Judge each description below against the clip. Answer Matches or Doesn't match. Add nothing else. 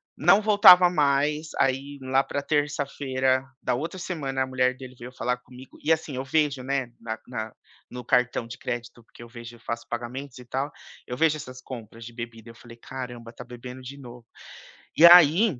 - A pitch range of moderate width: Matches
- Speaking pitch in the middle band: Doesn't match